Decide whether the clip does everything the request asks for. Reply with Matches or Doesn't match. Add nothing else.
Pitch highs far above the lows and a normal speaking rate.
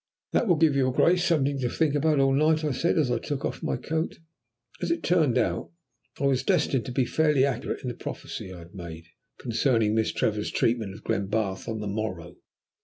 Doesn't match